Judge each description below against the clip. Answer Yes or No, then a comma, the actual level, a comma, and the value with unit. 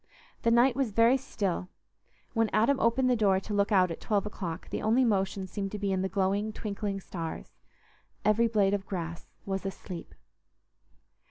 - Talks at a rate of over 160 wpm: Yes, average, 175 wpm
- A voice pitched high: Yes, high, 200 Hz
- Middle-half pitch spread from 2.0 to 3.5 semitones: Yes, average, 3.0 semitones